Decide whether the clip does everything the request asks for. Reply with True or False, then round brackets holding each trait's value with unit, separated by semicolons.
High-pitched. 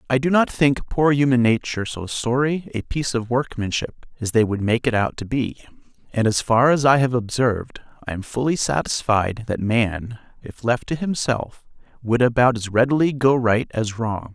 False (120 Hz)